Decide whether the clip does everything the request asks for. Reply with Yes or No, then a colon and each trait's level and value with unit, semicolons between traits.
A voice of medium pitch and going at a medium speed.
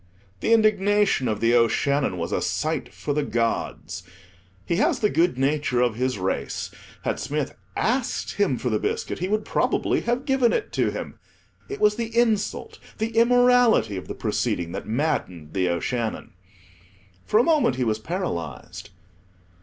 Yes: medium, 150 Hz; average, 160 wpm